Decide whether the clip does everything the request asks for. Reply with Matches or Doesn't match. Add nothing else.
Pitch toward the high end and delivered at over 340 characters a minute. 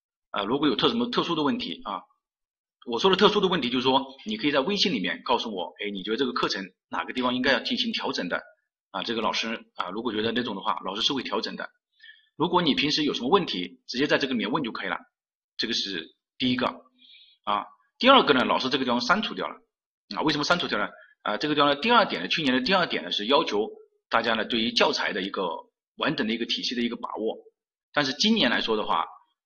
Matches